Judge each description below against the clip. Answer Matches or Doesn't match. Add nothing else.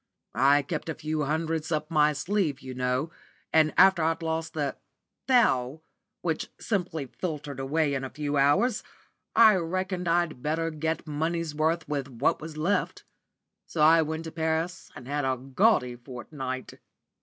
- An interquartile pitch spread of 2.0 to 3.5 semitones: Matches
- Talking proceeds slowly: Doesn't match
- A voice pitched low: Doesn't match